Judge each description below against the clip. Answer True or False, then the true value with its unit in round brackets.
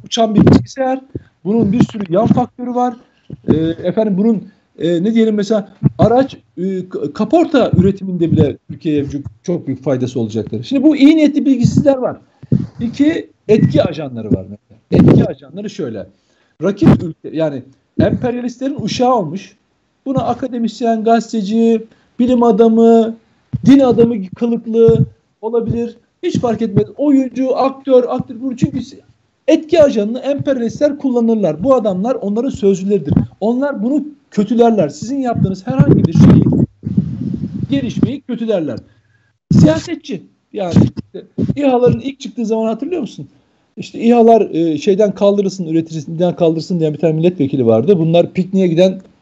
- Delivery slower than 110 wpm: False (125 wpm)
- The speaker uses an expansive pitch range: True (6.6 semitones)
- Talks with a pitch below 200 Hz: False (220 Hz)